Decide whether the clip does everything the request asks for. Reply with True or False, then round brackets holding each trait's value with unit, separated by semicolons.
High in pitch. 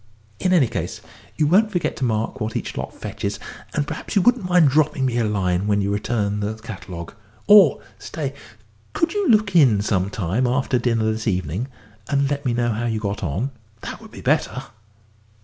False (120 Hz)